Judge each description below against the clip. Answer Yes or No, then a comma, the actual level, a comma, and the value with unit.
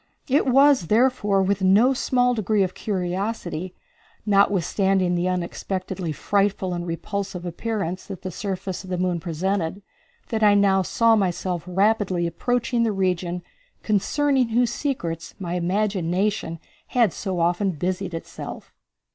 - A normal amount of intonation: Yes, average, 3.2 semitones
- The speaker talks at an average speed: No, slow, 130 wpm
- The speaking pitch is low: No, high, 190 Hz